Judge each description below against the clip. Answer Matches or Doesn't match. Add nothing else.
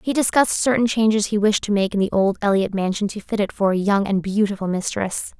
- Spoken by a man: Doesn't match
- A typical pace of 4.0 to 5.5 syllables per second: Doesn't match